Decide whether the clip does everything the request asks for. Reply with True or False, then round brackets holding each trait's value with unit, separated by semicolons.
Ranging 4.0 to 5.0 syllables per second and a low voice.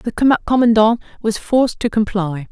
False (4.7 syllables/s; 220 Hz)